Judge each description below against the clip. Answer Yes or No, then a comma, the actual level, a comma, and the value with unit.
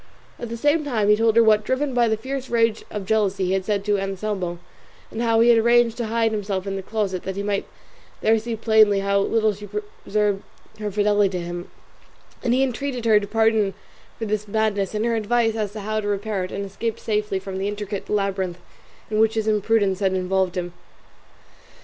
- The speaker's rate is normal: No, fast, 210 wpm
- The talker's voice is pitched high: Yes, high, 210 Hz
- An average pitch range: No, narrow, 2.3 semitones